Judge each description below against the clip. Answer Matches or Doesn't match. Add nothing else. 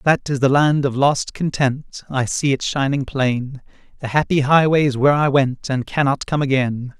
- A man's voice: Matches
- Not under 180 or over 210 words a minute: Matches